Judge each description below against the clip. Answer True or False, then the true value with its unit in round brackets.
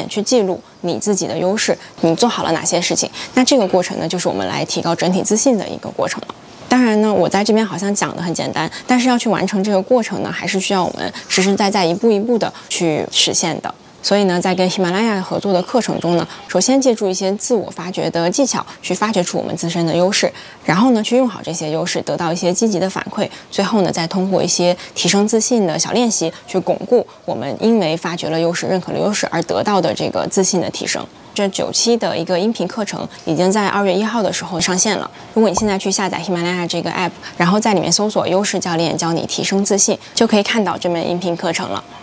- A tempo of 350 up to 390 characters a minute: True (365 characters per minute)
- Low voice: False (190 Hz)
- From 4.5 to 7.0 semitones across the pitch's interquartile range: False (3.3 semitones)